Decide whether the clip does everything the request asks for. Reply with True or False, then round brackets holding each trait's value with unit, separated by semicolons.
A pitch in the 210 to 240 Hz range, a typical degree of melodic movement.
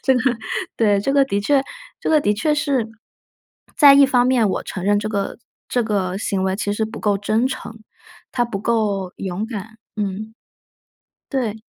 True (220 Hz; 4.1 semitones)